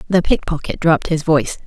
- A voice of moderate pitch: Yes, medium, 160 Hz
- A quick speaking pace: Yes, fast, 215 wpm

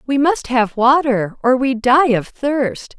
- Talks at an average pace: Yes, average, 180 wpm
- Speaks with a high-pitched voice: Yes, very high, 255 Hz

